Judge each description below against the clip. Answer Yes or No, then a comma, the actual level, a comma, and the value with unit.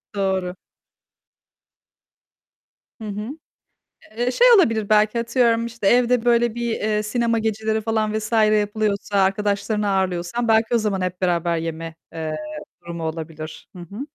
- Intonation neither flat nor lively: Yes, average, 3.5 semitones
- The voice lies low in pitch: No, high, 215 Hz